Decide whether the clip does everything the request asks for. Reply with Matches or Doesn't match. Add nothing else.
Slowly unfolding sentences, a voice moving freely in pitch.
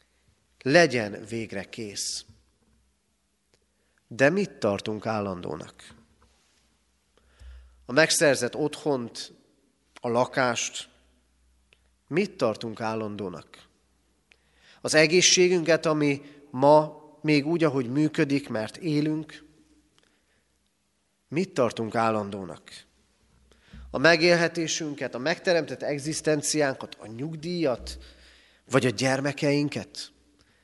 Matches